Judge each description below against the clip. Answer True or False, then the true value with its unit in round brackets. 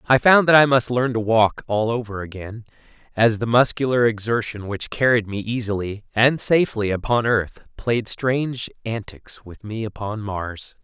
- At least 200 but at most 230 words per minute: False (165 wpm)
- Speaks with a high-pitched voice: False (115 Hz)